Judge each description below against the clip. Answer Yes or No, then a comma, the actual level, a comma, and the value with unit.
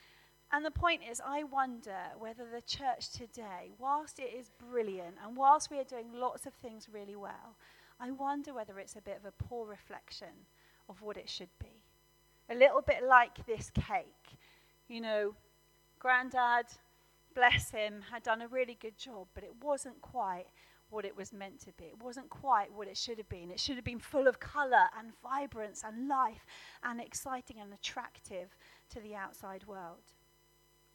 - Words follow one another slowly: No, average, 180 wpm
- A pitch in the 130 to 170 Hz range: No, high, 235 Hz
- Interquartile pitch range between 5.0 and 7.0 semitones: No, average, 4.1 semitones